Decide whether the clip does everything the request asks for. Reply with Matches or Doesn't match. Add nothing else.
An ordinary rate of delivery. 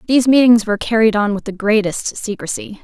Matches